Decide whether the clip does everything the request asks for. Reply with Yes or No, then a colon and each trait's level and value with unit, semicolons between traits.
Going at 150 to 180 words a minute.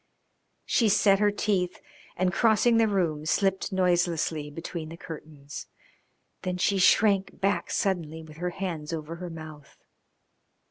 No: slow, 135 wpm